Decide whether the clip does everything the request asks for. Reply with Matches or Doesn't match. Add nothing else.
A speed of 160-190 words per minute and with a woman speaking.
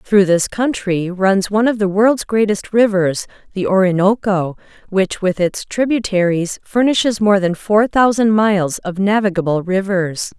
Doesn't match